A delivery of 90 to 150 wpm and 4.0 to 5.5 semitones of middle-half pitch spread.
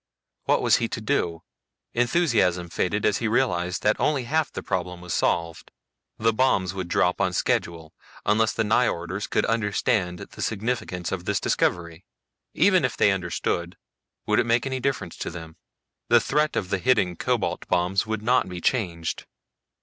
No: average, 170 wpm; average, 4.9 semitones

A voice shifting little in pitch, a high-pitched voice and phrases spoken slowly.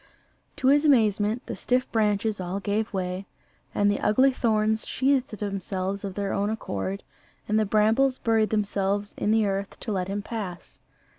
No: narrow, 2.1 semitones; high, 210 Hz; average, 165 wpm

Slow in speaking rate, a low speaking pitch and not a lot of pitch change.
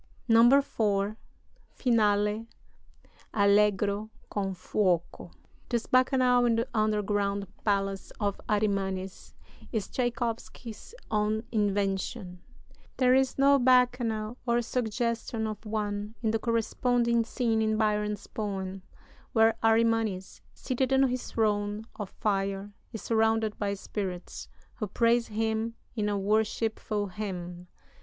No: slow, 110 wpm; high, 215 Hz; narrow, 2.3 semitones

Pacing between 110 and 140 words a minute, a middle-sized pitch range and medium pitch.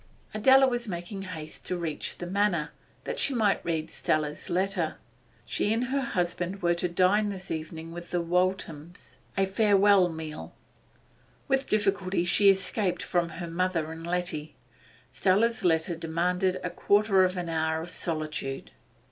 No: average, 150 wpm; average, 3.2 semitones; medium, 180 Hz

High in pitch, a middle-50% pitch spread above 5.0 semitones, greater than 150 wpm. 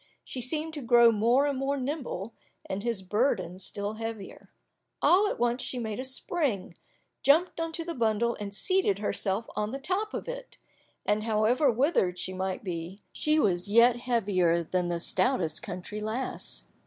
Yes: high, 230 Hz; wide, 5.5 semitones; average, 170 wpm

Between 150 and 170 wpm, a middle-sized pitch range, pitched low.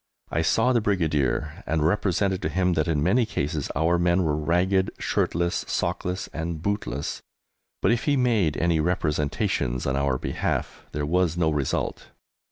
Yes: average, 160 wpm; average, 3.8 semitones; very low, 85 Hz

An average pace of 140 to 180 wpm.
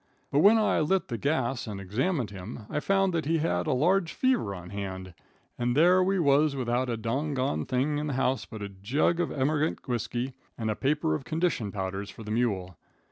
No: fast, 205 wpm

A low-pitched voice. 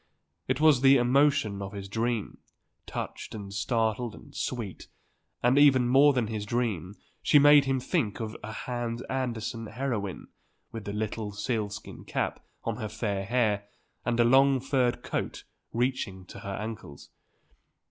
Yes: low, 115 Hz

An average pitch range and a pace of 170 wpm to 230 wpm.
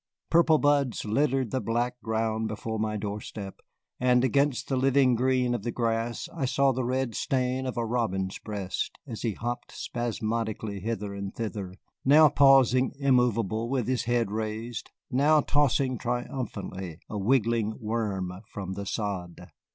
No: average, 3.4 semitones; average, 150 wpm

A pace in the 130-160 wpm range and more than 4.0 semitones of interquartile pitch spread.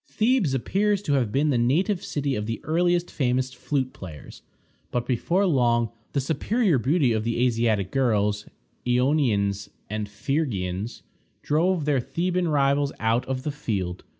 Yes: average, 150 wpm; wide, 5.4 semitones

